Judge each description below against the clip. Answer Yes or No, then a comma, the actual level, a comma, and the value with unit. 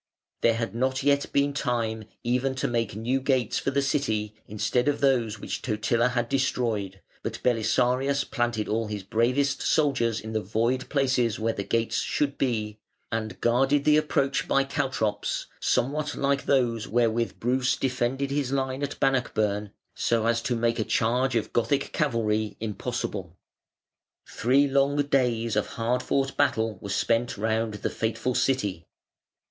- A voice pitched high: No, low, 120 Hz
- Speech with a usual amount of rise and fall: Yes, average, 3.5 semitones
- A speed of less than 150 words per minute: No, average, 155 wpm